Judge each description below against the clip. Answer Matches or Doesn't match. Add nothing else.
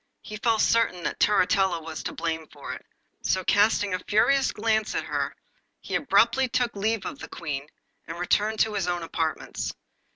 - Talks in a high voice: Matches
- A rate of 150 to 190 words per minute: Matches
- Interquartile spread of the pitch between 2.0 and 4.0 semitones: Doesn't match